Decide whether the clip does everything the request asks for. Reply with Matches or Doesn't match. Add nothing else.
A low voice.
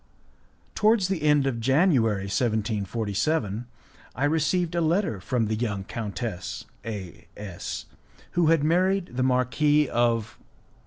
Matches